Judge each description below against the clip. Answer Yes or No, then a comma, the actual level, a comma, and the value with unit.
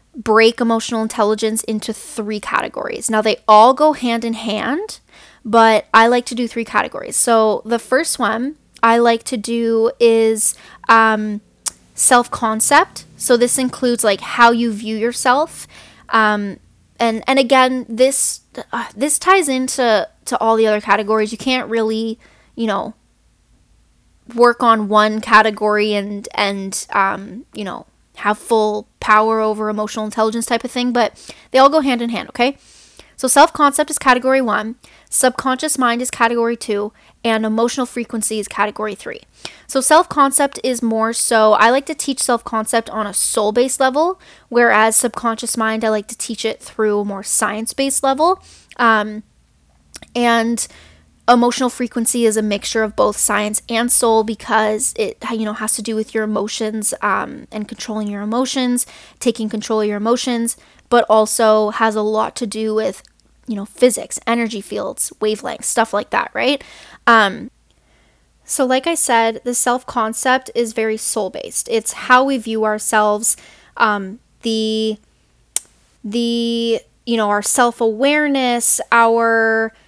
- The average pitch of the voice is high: Yes, high, 230 Hz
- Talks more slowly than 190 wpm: Yes, average, 155 wpm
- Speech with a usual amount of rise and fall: No, narrow, 2.3 semitones